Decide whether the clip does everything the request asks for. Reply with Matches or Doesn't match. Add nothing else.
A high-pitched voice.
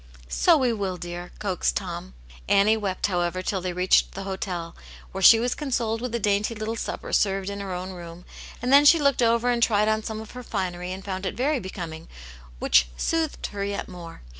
Matches